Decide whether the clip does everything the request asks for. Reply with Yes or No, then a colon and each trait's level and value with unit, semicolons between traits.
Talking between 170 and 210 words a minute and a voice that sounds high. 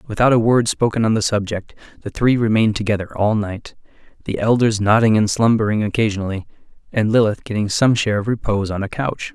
No: average, 185 wpm; low, 110 Hz